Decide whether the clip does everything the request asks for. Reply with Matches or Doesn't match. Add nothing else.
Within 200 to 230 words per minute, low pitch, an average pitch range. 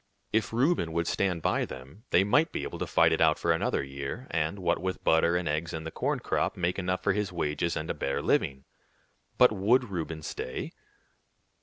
Matches